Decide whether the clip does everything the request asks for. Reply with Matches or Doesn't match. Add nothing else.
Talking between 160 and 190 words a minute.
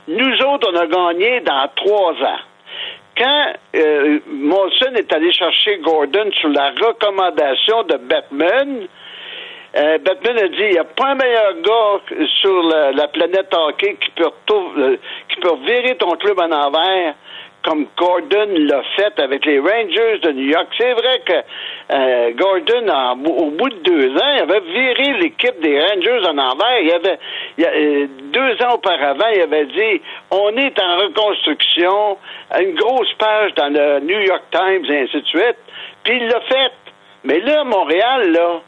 Matches